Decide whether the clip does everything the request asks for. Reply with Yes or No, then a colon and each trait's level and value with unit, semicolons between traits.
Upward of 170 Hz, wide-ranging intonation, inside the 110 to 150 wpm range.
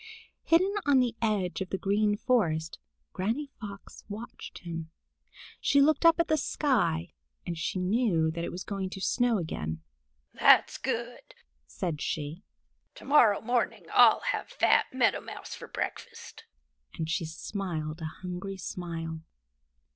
Yes: high, 190 Hz; wide, 6.5 semitones; average, 145 wpm